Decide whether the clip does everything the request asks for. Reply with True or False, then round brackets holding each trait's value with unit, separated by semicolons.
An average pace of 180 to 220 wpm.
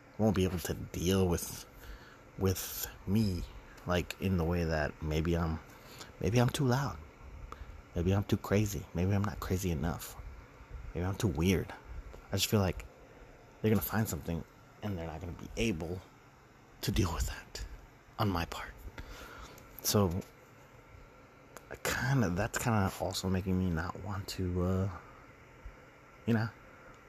False (155 wpm)